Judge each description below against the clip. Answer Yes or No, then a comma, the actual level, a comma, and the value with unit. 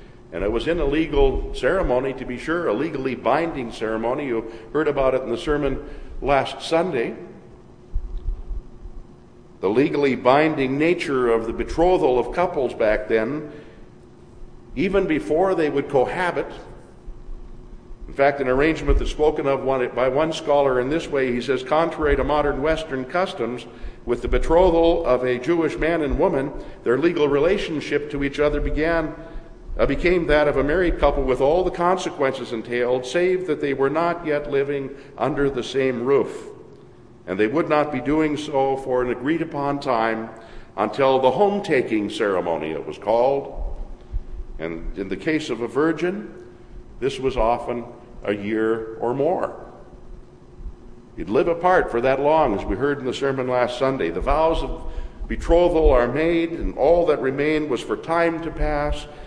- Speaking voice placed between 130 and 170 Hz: Yes, medium, 140 Hz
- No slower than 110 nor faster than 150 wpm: No, average, 160 wpm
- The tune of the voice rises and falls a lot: No, average, 4.6 semitones